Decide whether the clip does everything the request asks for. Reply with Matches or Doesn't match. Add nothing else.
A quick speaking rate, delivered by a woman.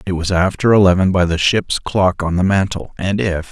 Doesn't match